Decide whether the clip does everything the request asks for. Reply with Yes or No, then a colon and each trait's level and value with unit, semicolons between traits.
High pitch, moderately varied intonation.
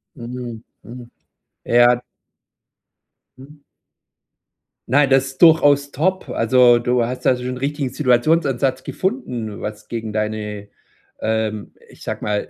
No: low, 125 Hz; average, 3.7 semitones